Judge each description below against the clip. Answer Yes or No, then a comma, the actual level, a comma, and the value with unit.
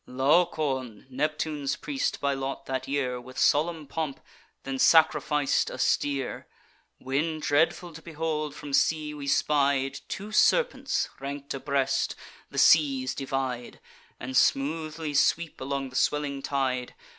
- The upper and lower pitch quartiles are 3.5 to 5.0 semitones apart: No, narrow, 2.5 semitones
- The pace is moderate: No, slow, 125 wpm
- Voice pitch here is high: No, medium, 140 Hz